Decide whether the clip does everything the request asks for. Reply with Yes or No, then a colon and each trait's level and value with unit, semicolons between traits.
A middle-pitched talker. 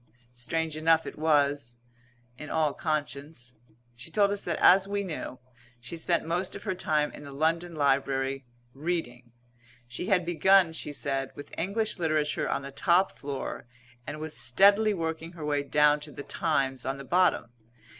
Yes: medium, 155 Hz